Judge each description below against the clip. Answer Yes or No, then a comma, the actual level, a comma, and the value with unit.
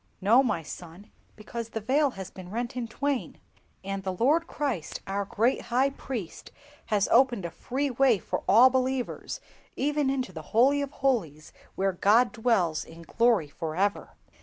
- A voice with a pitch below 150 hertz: No, high, 230 Hz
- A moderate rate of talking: Yes, average, 165 wpm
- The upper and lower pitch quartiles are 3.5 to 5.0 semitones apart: No, wide, 5.4 semitones